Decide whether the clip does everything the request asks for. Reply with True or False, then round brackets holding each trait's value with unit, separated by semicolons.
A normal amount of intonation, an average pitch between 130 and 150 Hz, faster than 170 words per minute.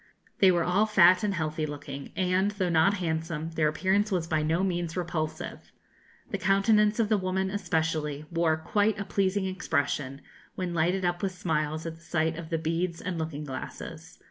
False (3.1 semitones; 170 Hz; 180 wpm)